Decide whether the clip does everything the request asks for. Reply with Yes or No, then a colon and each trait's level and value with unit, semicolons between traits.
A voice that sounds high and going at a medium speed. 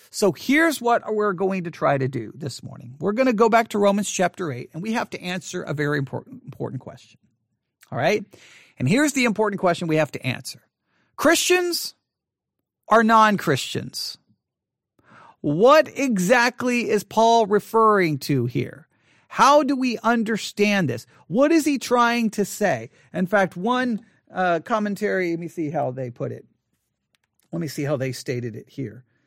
Yes: high, 200 Hz; average, 170 wpm